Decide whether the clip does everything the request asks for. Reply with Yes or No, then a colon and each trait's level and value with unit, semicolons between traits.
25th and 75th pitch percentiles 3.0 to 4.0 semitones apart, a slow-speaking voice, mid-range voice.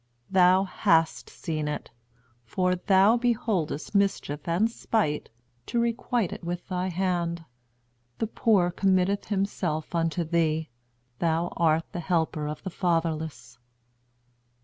Yes: average, 3.3 semitones; slow, 120 wpm; medium, 175 Hz